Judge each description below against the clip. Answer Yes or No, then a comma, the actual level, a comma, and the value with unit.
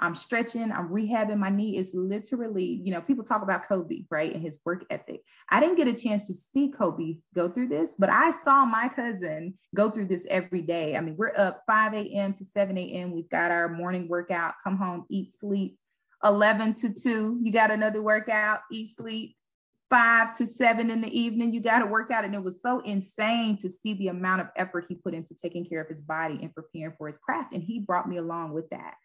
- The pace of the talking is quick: Yes, fast, 225 wpm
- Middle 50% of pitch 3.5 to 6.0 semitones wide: Yes, average, 4.2 semitones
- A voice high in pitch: Yes, high, 200 Hz